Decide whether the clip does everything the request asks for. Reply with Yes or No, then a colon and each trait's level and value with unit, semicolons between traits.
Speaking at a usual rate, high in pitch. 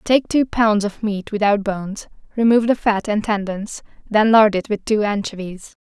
Yes: average, 185 wpm; high, 210 Hz